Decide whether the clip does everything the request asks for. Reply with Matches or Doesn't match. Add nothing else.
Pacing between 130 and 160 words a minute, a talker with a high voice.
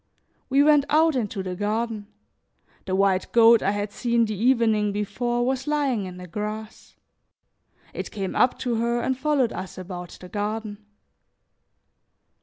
Matches